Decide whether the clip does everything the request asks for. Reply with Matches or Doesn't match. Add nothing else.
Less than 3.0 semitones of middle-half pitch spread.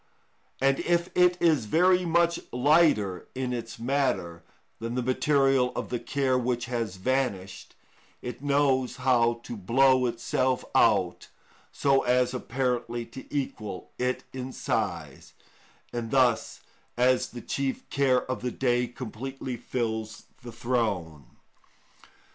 Matches